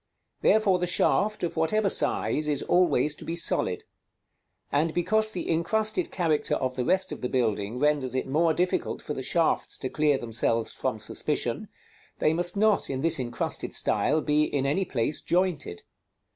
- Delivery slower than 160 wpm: No, average, 170 wpm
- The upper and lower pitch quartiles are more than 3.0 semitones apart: Yes, average, 5.2 semitones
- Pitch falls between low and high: Yes, medium, 155 Hz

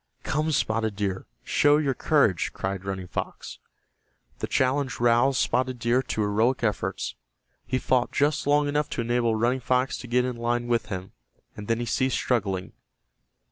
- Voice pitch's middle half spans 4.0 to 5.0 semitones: No, average, 3.2 semitones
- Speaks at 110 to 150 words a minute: No, average, 165 wpm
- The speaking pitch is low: Yes, low, 120 Hz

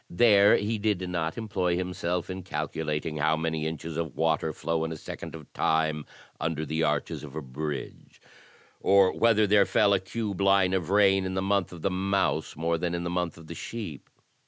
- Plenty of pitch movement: No, average, 3.5 semitones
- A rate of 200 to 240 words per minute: Yes, fast, 205 wpm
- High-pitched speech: No, very low, 85 Hz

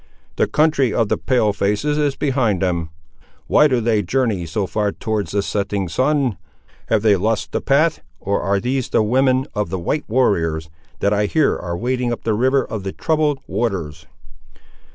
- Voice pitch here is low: Yes, low, 110 Hz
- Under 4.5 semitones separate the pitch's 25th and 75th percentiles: No, average, 5.0 semitones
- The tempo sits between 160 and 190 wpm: Yes, average, 180 wpm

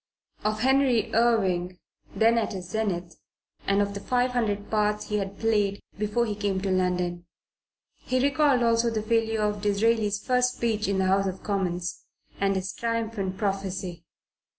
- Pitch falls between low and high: No, high, 210 Hz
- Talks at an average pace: Yes, average, 155 wpm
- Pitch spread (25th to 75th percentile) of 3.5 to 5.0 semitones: No, average, 3.1 semitones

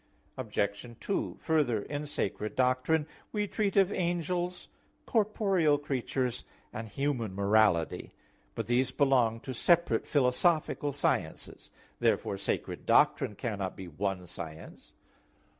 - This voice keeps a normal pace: No, slow, 110 wpm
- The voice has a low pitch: Yes, low, 130 Hz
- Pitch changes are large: Yes, wide, 7.4 semitones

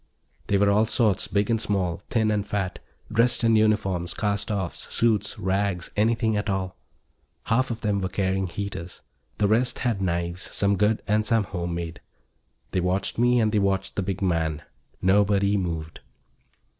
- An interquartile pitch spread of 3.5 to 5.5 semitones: No, narrow, 2.6 semitones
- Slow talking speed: No, average, 170 wpm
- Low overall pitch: Yes, low, 100 Hz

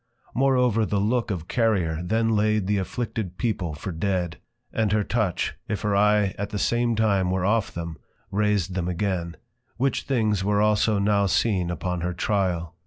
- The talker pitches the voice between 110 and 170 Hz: No, low, 100 Hz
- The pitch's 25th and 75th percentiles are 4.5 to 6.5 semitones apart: No, average, 3.2 semitones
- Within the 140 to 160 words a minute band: No, average, 175 wpm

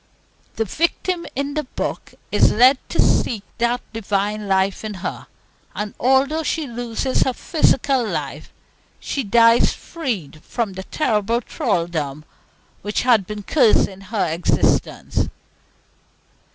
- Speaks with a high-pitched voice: Yes, high, 230 Hz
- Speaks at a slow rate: Yes, slow, 125 wpm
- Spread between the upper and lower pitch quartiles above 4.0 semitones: Yes, average, 5.0 semitones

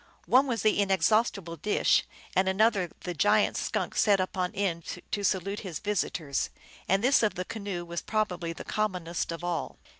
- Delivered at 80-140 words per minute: No, average, 175 wpm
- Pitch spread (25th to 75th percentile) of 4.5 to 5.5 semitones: No, average, 3.3 semitones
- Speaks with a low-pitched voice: No, high, 190 Hz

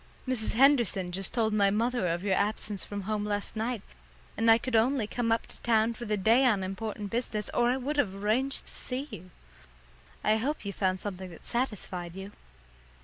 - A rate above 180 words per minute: Yes, average, 200 wpm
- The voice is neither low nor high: No, high, 215 Hz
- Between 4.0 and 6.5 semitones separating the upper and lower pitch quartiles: No, average, 3.4 semitones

